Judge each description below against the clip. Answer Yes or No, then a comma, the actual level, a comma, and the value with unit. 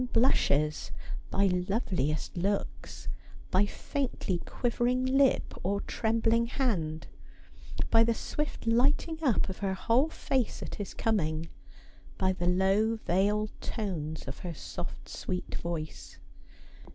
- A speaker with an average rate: No, slow, 115 wpm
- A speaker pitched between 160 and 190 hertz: No, high, 200 Hz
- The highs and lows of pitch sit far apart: No, average, 4.8 semitones